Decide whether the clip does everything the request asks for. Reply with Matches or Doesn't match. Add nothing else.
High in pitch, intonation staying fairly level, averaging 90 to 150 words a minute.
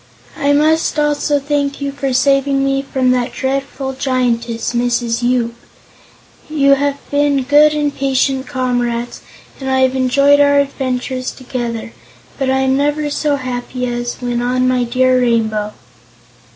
Matches